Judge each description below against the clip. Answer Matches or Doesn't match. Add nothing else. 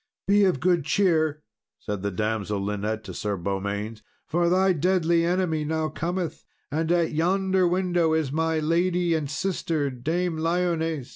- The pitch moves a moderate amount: Matches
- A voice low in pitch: Doesn't match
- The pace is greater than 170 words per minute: Doesn't match